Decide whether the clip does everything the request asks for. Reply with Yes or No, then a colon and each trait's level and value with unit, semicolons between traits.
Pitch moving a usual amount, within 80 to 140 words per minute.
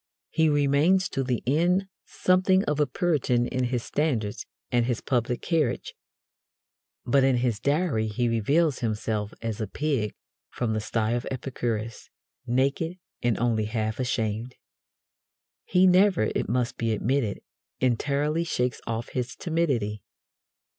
Yes: average, 4.7 semitones; slow, 135 wpm